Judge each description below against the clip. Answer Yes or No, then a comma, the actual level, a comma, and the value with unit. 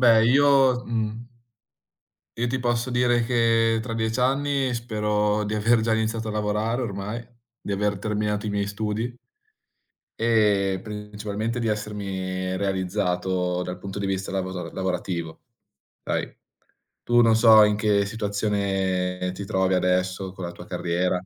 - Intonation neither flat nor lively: Yes, average, 3.0 semitones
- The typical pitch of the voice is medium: No, low, 105 Hz